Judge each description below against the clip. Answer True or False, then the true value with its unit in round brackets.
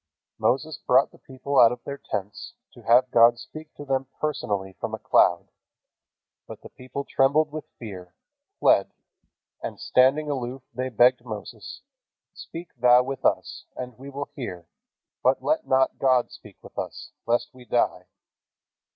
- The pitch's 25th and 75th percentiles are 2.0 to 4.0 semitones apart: True (2.8 semitones)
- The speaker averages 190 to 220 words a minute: False (155 wpm)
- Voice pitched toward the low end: True (130 Hz)